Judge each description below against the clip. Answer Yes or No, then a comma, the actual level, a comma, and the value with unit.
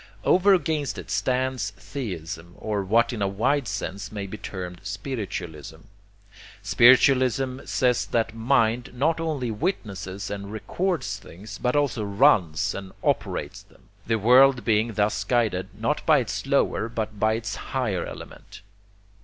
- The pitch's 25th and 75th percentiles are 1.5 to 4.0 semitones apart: No, average, 4.5 semitones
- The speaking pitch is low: Yes, low, 110 Hz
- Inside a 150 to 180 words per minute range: No, average, 140 wpm